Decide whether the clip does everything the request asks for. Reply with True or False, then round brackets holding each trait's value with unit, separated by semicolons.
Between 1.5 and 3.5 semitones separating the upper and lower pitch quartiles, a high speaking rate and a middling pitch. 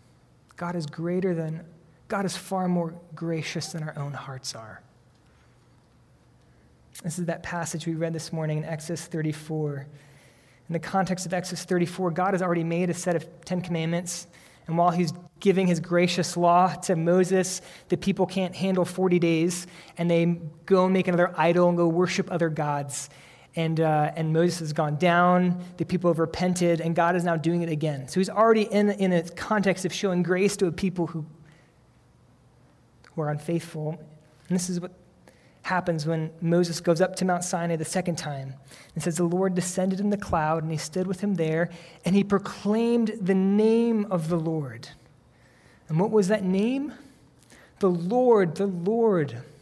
False (2.4 semitones; 180 wpm; 170 Hz)